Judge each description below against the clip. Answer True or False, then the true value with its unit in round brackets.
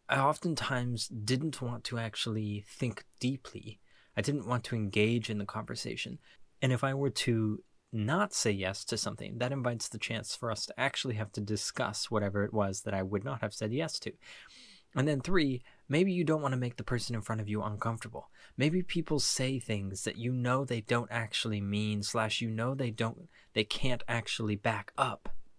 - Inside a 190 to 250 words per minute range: True (200 wpm)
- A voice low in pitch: True (115 Hz)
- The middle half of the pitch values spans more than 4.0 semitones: False (3.2 semitones)